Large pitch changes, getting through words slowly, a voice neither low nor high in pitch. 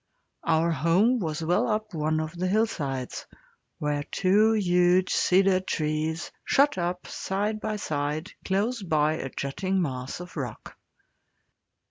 No: average, 4.2 semitones; slow, 130 wpm; medium, 175 Hz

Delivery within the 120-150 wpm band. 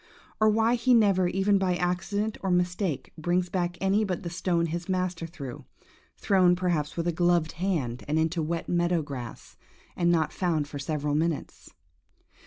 No: average, 170 wpm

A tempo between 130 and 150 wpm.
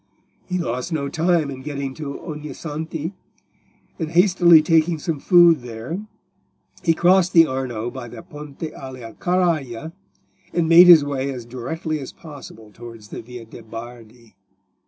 Yes: average, 145 wpm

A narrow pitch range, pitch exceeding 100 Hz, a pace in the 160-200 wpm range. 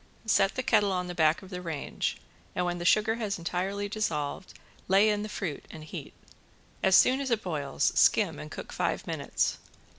No: average, 3.7 semitones; high, 190 Hz; average, 190 wpm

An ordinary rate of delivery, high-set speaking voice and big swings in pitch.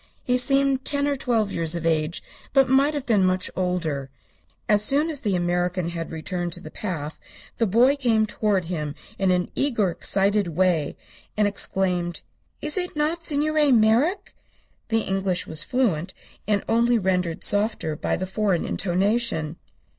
Yes: average, 160 wpm; high, 200 Hz; wide, 6.0 semitones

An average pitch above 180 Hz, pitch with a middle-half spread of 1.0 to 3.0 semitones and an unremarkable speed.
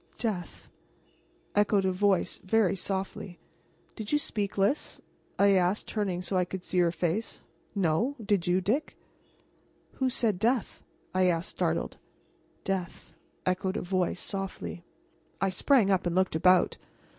Yes: high, 190 Hz; narrow, 2.4 semitones; average, 145 wpm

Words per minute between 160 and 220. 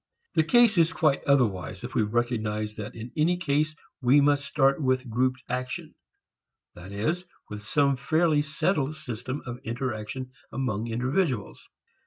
No: average, 145 wpm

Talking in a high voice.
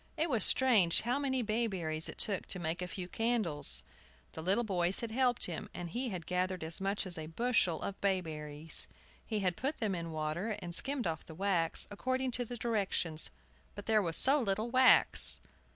Yes: high, 195 Hz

